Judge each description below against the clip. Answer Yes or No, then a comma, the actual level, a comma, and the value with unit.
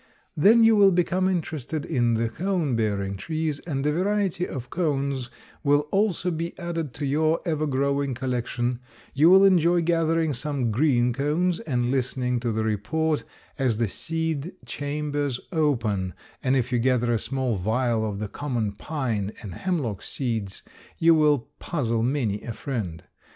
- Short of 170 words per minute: Yes, average, 155 wpm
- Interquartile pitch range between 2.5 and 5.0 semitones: No, wide, 5.4 semitones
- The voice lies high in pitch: No, medium, 140 Hz